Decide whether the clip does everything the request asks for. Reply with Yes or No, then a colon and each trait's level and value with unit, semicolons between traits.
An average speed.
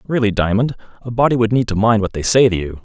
No: fast, 275 wpm